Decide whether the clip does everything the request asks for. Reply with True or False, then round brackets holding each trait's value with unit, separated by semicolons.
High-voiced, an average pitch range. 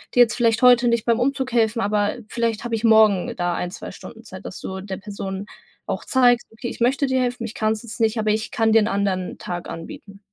True (225 Hz; 3.0 semitones)